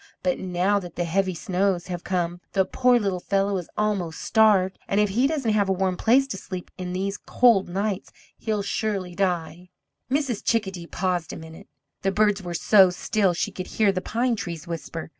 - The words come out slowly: No, average, 195 wpm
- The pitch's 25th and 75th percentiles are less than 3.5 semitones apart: Yes, average, 2.8 semitones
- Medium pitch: No, high, 195 Hz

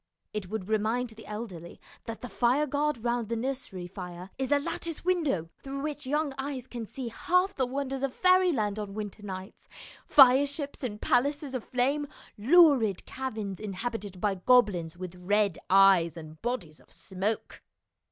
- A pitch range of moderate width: No, wide, 5.7 semitones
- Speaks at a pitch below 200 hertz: No, high, 230 Hz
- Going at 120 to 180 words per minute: Yes, average, 155 wpm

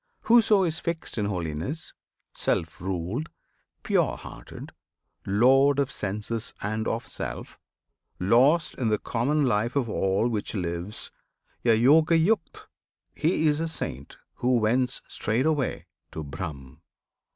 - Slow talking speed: Yes, slow, 120 wpm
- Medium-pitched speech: No, low, 115 Hz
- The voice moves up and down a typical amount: No, wide, 7.1 semitones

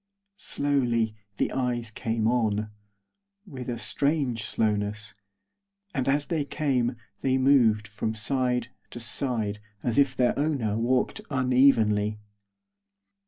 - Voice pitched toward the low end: Yes, low, 120 Hz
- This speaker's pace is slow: Yes, slow, 115 wpm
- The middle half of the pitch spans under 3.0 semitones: No, average, 3.7 semitones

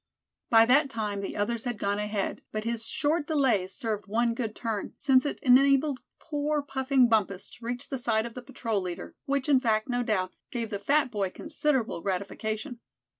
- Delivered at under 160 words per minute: No, average, 180 wpm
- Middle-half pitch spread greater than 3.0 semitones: Yes, average, 4.1 semitones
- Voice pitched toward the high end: Yes, high, 235 Hz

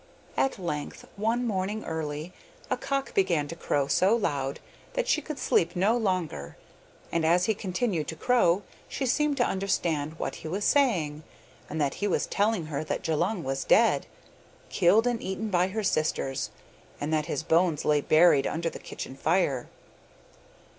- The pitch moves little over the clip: No, wide, 5.5 semitones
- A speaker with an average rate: Yes, average, 165 wpm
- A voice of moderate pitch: Yes, medium, 175 Hz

